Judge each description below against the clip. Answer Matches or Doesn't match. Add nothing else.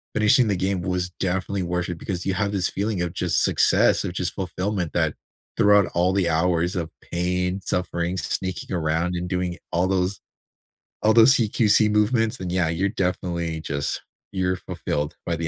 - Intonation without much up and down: Matches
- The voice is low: Matches